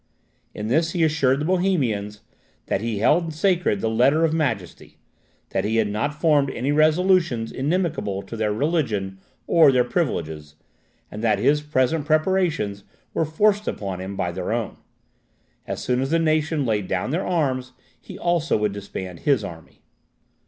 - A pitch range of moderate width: No, wide, 7.3 semitones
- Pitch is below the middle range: Yes, low, 130 Hz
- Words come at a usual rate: Yes, average, 160 wpm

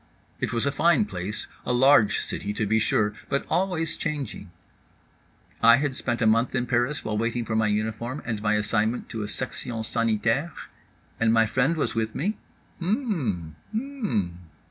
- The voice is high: No, low, 115 Hz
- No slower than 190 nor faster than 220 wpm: No, average, 170 wpm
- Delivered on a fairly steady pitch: No, average, 4.9 semitones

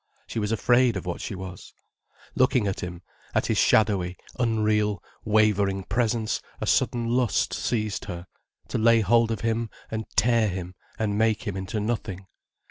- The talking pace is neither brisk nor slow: Yes, average, 160 wpm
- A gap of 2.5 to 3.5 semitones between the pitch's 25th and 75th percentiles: Yes, average, 2.9 semitones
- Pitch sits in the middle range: No, low, 110 Hz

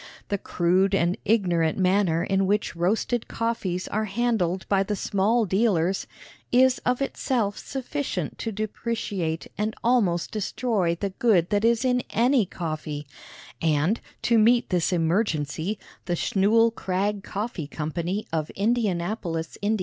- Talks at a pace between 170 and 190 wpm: No, slow, 135 wpm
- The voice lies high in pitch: Yes, high, 200 Hz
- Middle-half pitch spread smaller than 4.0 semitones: No, average, 4.7 semitones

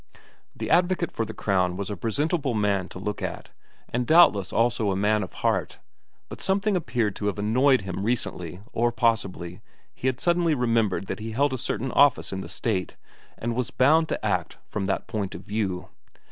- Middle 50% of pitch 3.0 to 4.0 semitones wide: No, average, 4.9 semitones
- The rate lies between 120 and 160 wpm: No, average, 190 wpm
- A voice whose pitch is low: Yes, low, 110 Hz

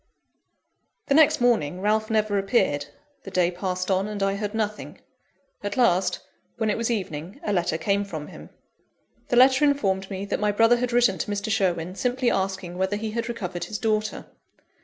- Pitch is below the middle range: No, high, 205 Hz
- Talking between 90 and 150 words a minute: No, average, 180 wpm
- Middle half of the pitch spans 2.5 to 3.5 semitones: Yes, average, 3.2 semitones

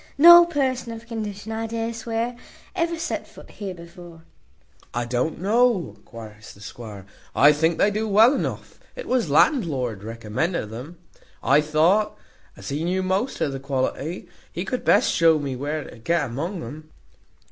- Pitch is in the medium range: Yes, medium, 170 Hz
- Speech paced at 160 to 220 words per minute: Yes, average, 165 wpm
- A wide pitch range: Yes, wide, 8.4 semitones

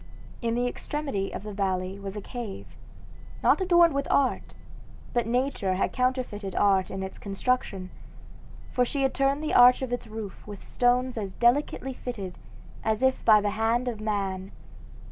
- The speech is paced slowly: No, average, 165 wpm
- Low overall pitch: No, high, 230 Hz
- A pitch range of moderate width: Yes, average, 4.4 semitones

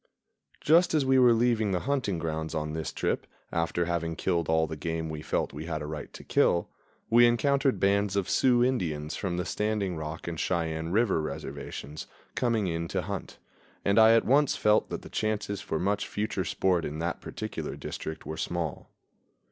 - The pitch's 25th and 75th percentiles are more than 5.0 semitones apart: Yes, wide, 5.5 semitones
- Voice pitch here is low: Yes, very low, 90 Hz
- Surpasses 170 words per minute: Yes, average, 190 wpm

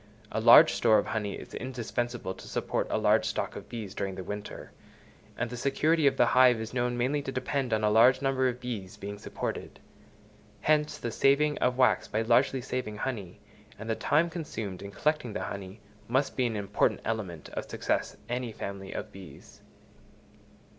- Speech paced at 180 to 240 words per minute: Yes, average, 185 wpm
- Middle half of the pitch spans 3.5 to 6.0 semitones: Yes, average, 4.0 semitones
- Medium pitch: No, low, 120 Hz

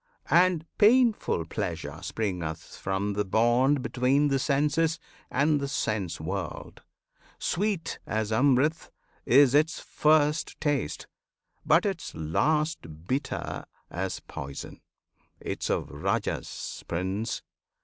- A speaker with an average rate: No, slow, 105 wpm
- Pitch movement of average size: No, wide, 8.1 semitones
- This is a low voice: Yes, low, 130 Hz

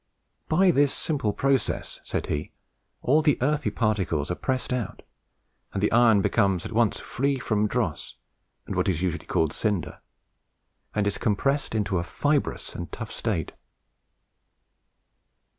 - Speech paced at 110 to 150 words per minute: Yes, average, 140 wpm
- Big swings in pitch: Yes, wide, 6.1 semitones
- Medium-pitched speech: No, low, 110 Hz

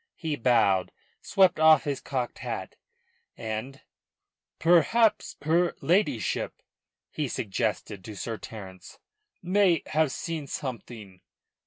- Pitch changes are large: Yes, wide, 7.1 semitones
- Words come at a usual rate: No, slow, 105 wpm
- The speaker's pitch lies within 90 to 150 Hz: Yes, medium, 140 Hz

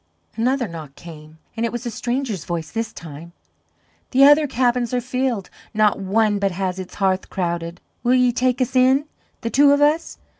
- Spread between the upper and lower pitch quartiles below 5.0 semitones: No, wide, 5.6 semitones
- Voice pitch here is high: Yes, high, 230 Hz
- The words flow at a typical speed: Yes, average, 185 wpm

